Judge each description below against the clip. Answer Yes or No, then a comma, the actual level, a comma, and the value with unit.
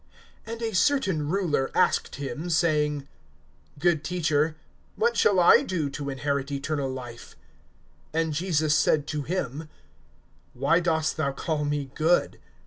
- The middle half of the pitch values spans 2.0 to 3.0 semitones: No, average, 3.4 semitones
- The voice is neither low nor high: Yes, medium, 155 Hz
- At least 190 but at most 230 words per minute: No, slow, 135 wpm